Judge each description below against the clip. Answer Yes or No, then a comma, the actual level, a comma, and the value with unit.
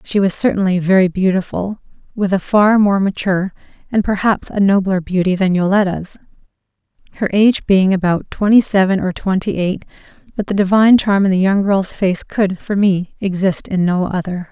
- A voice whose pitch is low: No, high, 190 Hz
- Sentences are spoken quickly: No, average, 175 wpm